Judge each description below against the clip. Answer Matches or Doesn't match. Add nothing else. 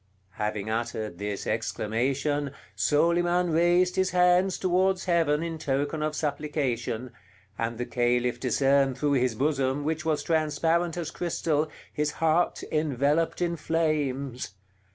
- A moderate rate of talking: Doesn't match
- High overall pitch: Doesn't match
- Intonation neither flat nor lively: Matches